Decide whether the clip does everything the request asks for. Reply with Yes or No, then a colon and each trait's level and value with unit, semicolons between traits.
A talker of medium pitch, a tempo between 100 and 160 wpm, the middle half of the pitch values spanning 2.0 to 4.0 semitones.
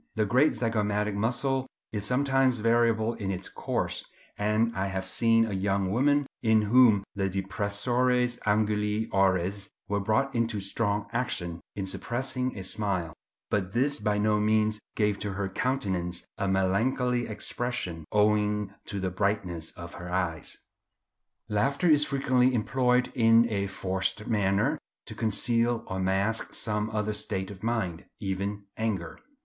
No: low, 105 Hz; average, 145 wpm; average, 3.3 semitones